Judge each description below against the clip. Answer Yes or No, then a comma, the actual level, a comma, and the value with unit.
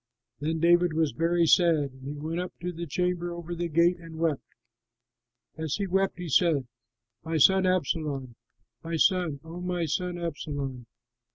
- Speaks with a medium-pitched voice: Yes, medium, 165 Hz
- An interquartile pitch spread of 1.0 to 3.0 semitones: Yes, narrow, 2.4 semitones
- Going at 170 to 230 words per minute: No, average, 160 wpm